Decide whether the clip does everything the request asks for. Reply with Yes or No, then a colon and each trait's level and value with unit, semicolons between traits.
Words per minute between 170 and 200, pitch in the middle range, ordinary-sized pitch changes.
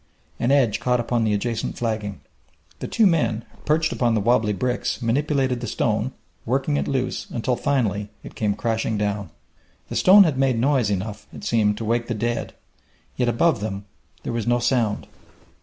No: average, 175 wpm; low, 120 Hz; average, 3.3 semitones